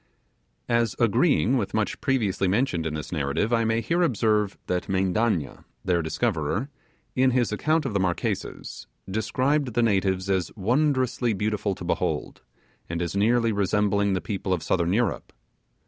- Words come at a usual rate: Yes, average, 150 wpm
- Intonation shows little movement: No, average, 4.3 semitones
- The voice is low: Yes, low, 105 Hz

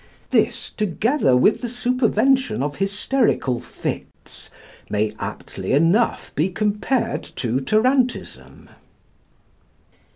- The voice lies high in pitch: Yes, high, 210 Hz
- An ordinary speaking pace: No, slow, 90 wpm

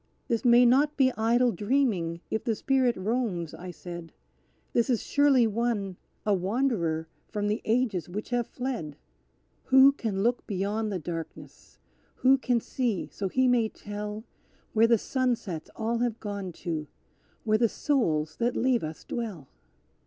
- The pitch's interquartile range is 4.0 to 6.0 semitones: Yes, average, 4.8 semitones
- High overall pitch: Yes, high, 225 Hz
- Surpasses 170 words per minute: No, average, 150 wpm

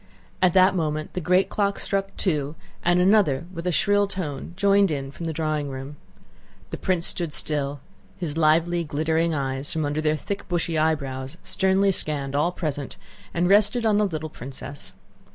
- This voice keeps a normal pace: Yes, average, 170 wpm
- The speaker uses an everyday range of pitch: Yes, average, 4.1 semitones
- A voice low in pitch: No, medium, 160 Hz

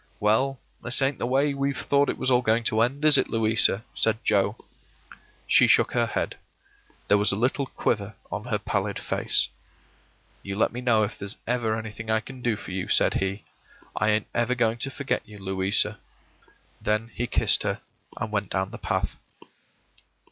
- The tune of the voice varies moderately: Yes, average, 3.2 semitones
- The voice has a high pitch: No, low, 110 Hz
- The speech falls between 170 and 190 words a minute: Yes, average, 185 wpm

